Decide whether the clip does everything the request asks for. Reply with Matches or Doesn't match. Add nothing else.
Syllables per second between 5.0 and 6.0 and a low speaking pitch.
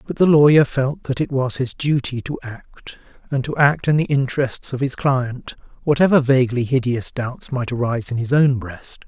Matches